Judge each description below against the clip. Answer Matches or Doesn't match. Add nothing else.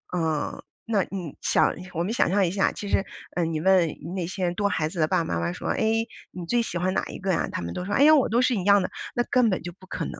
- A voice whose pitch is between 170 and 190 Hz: Matches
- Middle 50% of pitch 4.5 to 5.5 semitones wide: Doesn't match